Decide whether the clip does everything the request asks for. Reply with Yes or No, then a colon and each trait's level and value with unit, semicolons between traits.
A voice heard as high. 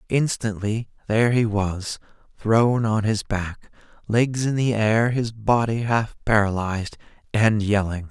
No: low, 110 Hz